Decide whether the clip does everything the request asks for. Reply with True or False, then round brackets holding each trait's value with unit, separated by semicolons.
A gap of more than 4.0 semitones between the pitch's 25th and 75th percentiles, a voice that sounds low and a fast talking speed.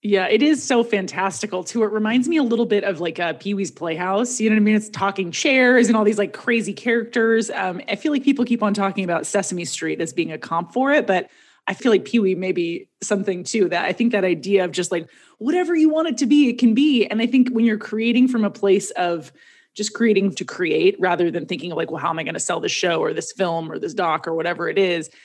False (4.4 semitones; 205 Hz; 265 wpm)